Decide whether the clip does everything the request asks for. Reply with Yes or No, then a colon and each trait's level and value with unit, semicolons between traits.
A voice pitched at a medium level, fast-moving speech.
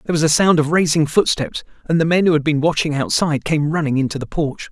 Yes: medium, 155 Hz; fast, 255 wpm